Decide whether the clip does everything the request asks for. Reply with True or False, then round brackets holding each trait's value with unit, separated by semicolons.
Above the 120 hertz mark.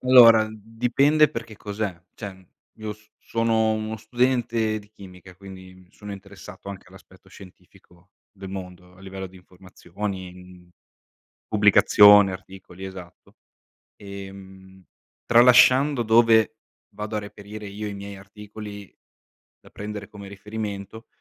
False (100 Hz)